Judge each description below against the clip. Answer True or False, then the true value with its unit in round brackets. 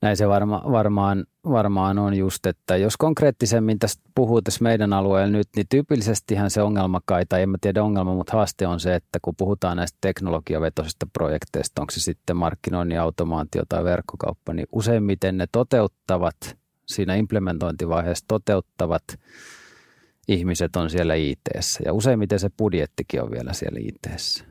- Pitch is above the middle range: False (95 Hz)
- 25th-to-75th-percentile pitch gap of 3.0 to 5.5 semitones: True (3.3 semitones)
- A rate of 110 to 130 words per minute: False (150 wpm)